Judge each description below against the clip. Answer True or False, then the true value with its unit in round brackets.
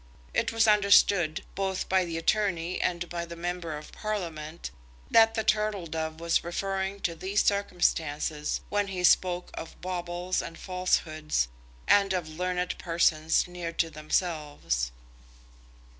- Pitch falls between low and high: True (175 Hz)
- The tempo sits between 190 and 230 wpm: False (135 wpm)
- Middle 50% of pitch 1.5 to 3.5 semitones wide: True (2.8 semitones)